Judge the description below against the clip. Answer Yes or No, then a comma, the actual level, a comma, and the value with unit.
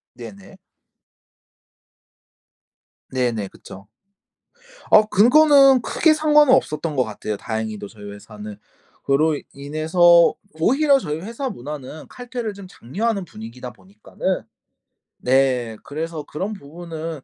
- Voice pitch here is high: No, medium, 155 Hz